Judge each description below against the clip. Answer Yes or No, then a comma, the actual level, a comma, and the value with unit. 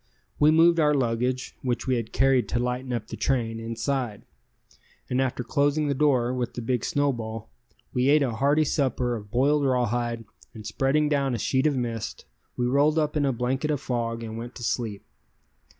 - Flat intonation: No, average, 3.2 semitones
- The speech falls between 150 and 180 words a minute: No, average, 190 wpm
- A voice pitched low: Yes, low, 125 Hz